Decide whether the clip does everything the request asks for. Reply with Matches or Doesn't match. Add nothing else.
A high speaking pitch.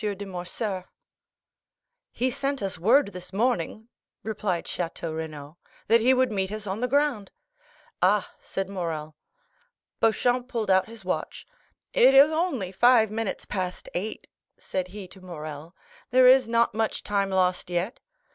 Matches